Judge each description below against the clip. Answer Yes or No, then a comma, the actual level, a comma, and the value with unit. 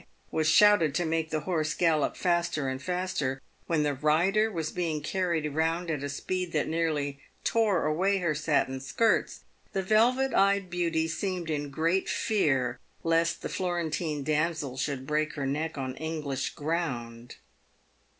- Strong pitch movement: No, average, 3.3 semitones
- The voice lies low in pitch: No, medium, 160 Hz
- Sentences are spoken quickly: No, average, 150 wpm